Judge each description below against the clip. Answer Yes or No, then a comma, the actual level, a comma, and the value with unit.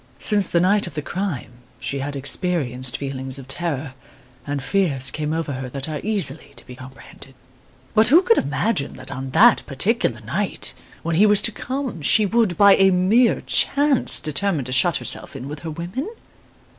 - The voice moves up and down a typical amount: No, wide, 7.0 semitones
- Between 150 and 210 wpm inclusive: Yes, average, 180 wpm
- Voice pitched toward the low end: No, medium, 160 Hz